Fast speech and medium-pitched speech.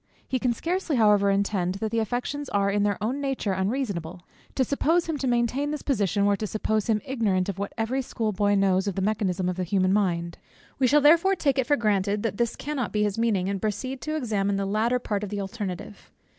No: fast, 225 wpm; high, 215 Hz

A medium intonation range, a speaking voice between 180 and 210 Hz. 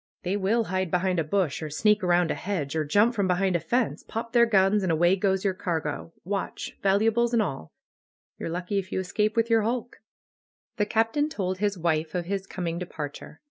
Yes: average, 3.4 semitones; high, 190 Hz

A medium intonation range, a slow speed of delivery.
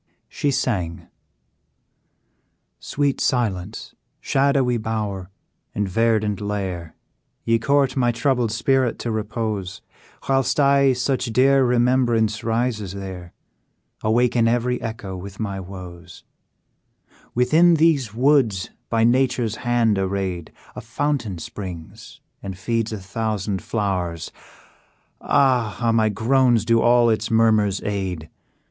Yes: average, 4.1 semitones; slow, 110 wpm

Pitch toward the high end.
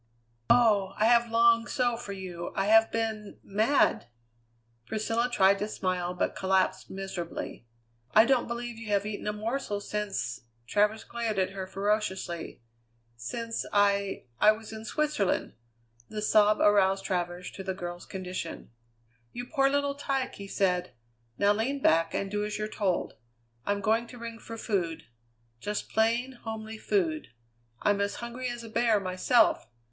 Yes: high, 210 Hz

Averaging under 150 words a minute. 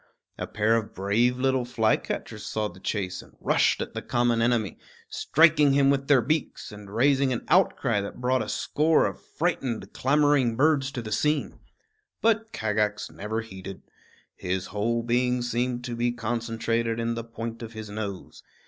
No: average, 165 wpm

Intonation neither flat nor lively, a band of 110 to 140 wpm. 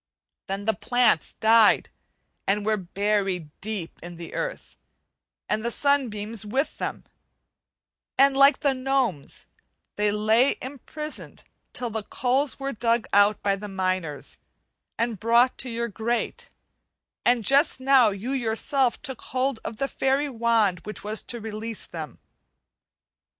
Yes: average, 4.1 semitones; slow, 135 wpm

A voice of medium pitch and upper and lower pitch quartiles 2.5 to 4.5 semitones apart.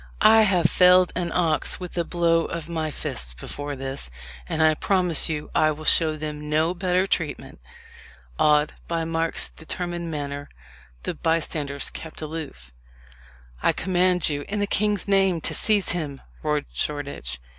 Yes: medium, 160 Hz; average, 3.0 semitones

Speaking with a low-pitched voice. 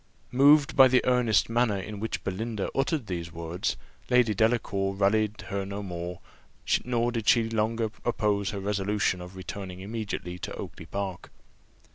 Yes: low, 105 Hz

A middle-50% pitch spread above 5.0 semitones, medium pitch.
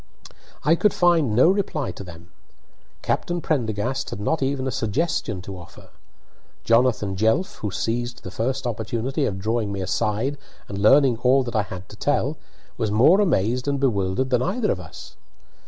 No: wide, 5.4 semitones; low, 120 Hz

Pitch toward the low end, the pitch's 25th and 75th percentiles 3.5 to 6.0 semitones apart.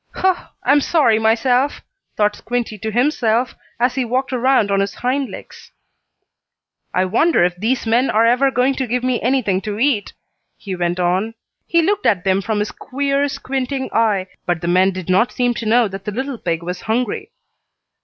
No: high, 230 Hz; average, 4.8 semitones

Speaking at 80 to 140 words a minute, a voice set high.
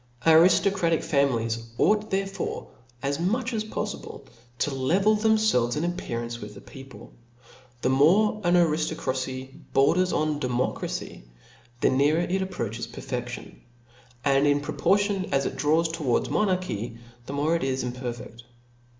No: slow, 135 wpm; medium, 145 Hz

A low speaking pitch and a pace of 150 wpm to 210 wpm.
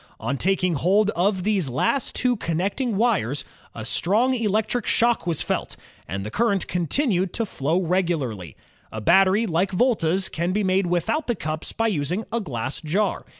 No: medium, 185 Hz; average, 170 wpm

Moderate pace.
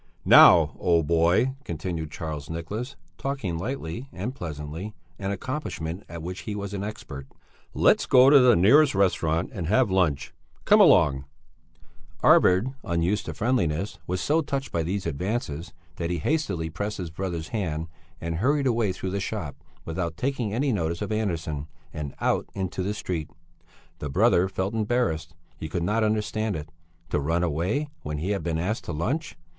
Yes: average, 165 wpm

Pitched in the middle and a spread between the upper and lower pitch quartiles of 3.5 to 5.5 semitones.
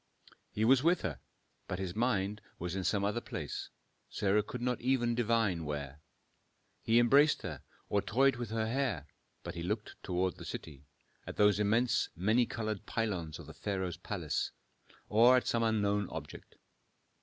No: low, 105 Hz; average, 4.3 semitones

